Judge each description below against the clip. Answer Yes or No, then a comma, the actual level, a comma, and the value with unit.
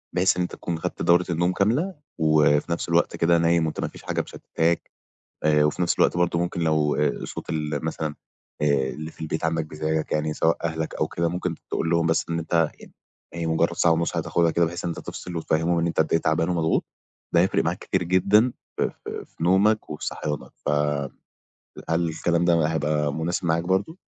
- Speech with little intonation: Yes, narrow, 1.6 semitones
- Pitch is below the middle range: Yes, very low, 85 Hz